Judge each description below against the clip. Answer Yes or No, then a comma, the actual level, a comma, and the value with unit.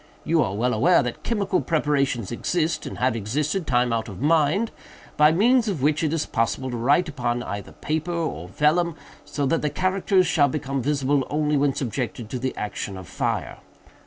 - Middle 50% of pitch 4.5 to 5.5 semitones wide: Yes, average, 5.1 semitones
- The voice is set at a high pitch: No, medium, 145 Hz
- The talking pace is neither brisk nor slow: Yes, average, 190 wpm